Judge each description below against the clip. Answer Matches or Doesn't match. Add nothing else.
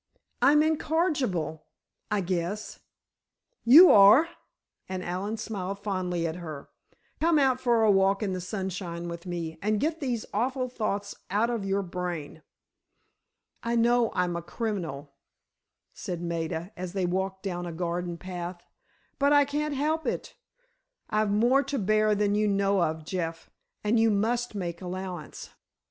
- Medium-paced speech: Matches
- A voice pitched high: Matches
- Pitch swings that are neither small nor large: Matches